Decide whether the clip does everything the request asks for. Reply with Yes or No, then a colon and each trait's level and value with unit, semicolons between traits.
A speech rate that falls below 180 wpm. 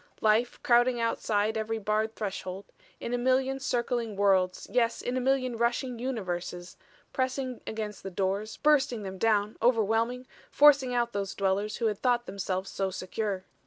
Yes: average, 155 wpm